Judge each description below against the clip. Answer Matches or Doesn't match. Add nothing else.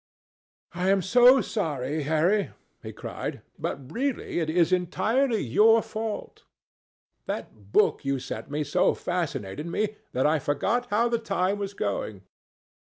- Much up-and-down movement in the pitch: Matches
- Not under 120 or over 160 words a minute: Matches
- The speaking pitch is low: Doesn't match